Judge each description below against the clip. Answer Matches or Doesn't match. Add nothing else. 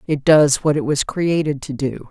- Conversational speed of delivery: Doesn't match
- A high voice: Doesn't match